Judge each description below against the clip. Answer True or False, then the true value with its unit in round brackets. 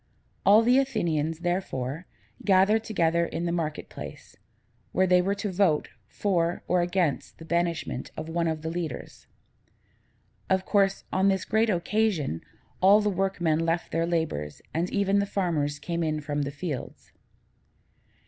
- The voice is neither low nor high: True (175 Hz)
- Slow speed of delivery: False (150 wpm)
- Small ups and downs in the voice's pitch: False (3.4 semitones)